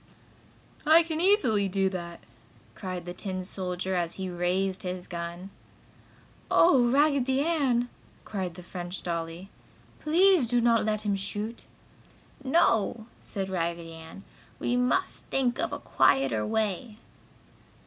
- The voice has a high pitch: Yes, high, 195 Hz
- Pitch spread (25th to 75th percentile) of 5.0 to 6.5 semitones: Yes, wide, 5.6 semitones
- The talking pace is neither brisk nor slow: No, slow, 130 wpm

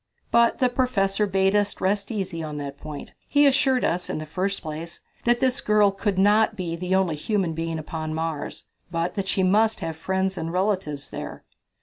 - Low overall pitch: No, high, 190 Hz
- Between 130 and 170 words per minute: No, average, 200 wpm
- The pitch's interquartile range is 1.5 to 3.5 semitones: No, average, 4.2 semitones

